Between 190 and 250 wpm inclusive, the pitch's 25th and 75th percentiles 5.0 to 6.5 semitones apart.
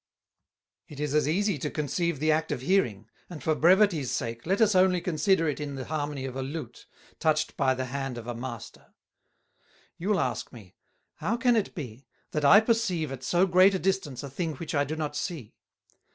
Yes: average, 200 wpm; wide, 5.5 semitones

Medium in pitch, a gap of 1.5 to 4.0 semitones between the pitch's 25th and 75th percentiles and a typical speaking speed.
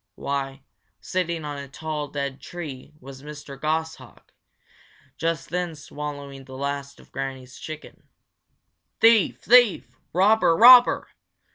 No: medium, 150 Hz; average, 3.5 semitones; slow, 115 wpm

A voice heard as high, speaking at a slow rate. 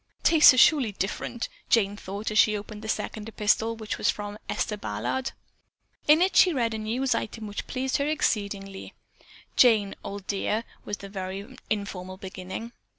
No: high, 215 Hz; average, 165 wpm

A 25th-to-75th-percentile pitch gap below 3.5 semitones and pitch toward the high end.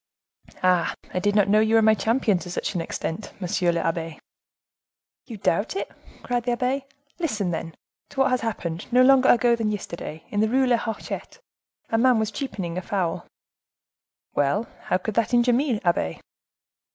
No: average, 5.2 semitones; high, 215 Hz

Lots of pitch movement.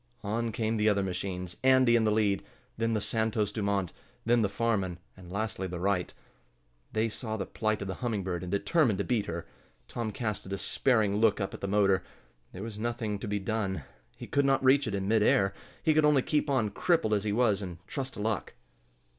No: average, 2.9 semitones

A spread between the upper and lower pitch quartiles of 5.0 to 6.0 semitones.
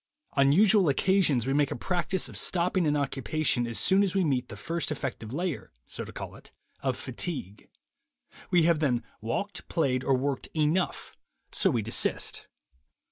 Yes: wide, 5.5 semitones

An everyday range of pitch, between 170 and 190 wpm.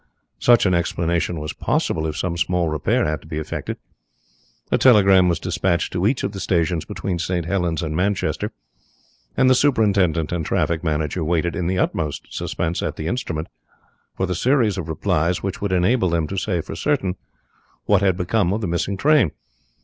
Yes: average, 3.2 semitones; average, 185 wpm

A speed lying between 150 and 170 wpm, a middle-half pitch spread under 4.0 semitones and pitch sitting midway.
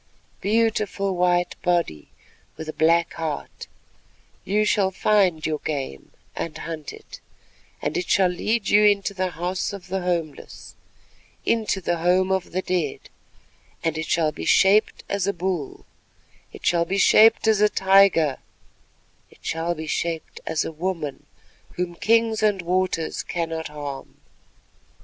No: average, 140 wpm; average, 3.5 semitones; medium, 180 Hz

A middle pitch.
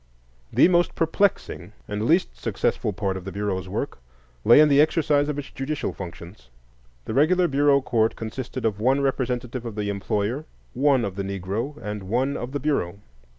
No: low, 120 Hz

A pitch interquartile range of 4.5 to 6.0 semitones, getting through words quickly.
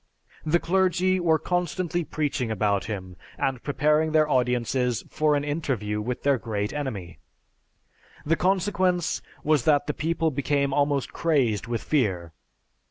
No: average, 5.2 semitones; slow, 135 wpm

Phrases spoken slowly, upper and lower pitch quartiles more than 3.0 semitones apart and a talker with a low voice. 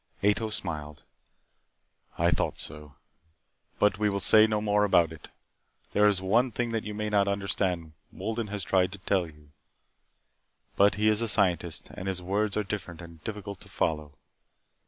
No: average, 170 wpm; average, 3.5 semitones; low, 100 Hz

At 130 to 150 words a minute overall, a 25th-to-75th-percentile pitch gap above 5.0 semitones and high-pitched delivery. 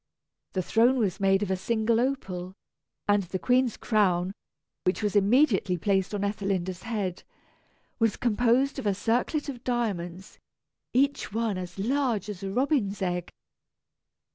No: average, 140 wpm; average, 4.1 semitones; high, 205 Hz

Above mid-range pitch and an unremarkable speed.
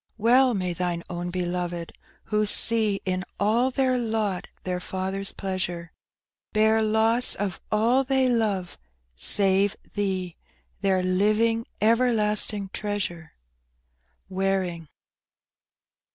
No: high, 200 Hz; slow, 105 wpm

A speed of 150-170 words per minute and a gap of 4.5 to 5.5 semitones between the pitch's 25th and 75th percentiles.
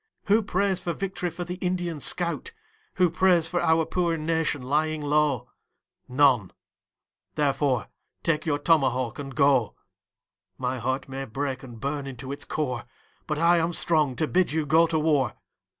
No: average, 160 wpm; average, 3.9 semitones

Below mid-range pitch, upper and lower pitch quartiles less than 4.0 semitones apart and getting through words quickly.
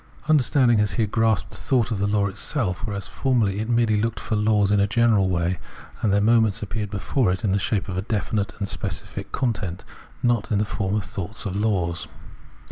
Yes: low, 105 Hz; narrow, 2.5 semitones; fast, 210 wpm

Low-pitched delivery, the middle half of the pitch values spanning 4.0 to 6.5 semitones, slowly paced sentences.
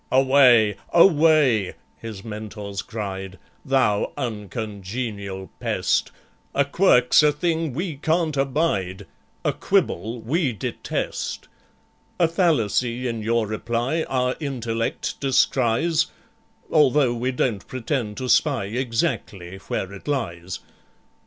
Yes: low, 120 Hz; average, 5.2 semitones; slow, 105 wpm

